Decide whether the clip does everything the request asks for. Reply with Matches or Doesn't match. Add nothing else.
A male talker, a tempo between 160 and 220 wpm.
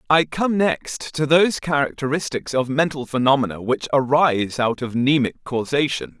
Doesn't match